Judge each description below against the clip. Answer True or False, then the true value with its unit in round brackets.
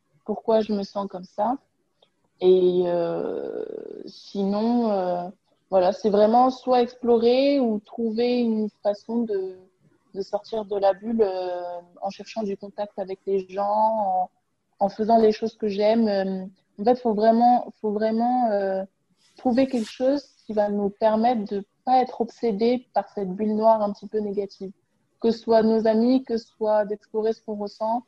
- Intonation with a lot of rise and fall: False (2.8 semitones)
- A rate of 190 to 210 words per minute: False (175 wpm)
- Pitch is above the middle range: True (215 Hz)